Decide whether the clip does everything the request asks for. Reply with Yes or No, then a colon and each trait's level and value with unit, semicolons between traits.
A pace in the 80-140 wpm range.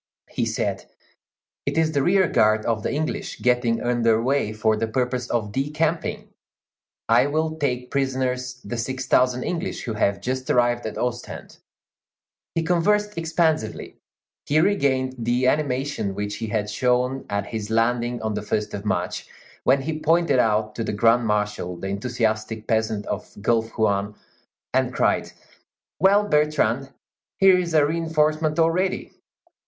No: average, 150 wpm